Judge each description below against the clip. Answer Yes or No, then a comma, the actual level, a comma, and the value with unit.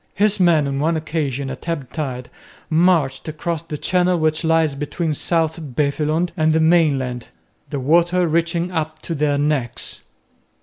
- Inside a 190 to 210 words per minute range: No, average, 155 wpm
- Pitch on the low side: No, medium, 155 Hz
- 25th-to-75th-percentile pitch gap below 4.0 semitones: Yes, average, 2.9 semitones